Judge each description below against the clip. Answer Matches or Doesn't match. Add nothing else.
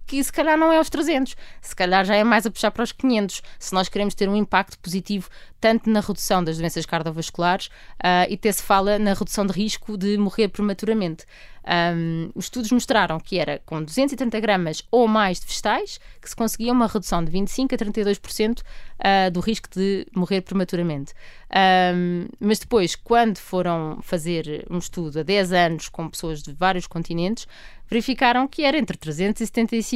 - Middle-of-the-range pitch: Doesn't match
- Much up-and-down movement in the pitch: Doesn't match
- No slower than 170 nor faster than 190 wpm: Matches